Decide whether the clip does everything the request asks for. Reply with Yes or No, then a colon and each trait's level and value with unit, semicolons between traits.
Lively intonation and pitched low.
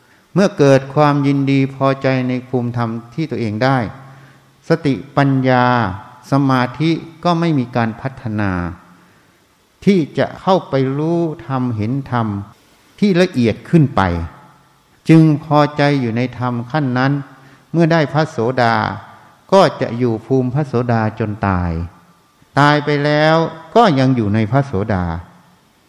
No: average, 4.2 semitones; low, 130 Hz